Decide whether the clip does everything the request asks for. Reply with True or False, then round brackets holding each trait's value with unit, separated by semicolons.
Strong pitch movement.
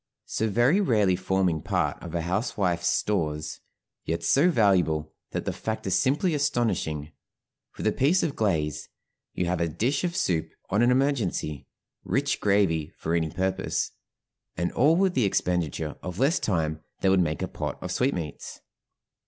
True (7.2 semitones)